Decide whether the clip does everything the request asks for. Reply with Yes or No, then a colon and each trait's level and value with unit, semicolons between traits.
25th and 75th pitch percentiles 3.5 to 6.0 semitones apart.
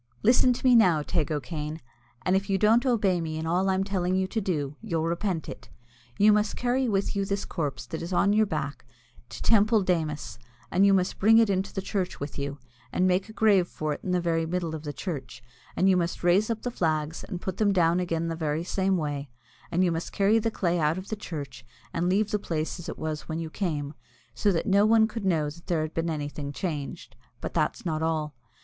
Yes: average, 4.1 semitones